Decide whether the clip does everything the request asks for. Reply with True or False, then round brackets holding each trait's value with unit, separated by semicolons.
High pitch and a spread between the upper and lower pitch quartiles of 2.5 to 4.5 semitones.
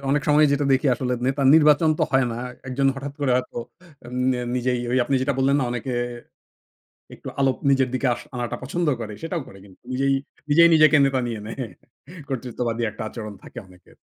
False (130 Hz; 2.8 semitones)